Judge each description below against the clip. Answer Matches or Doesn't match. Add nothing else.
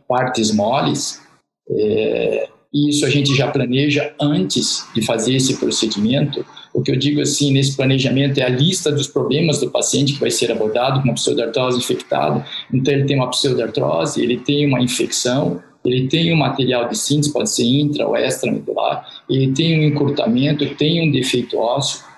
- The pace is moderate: Matches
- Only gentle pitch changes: Matches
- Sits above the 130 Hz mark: Matches